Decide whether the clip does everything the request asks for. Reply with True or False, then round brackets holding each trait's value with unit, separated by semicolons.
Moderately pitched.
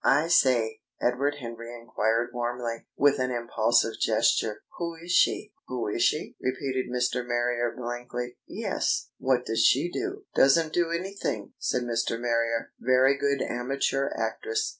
False (125 Hz)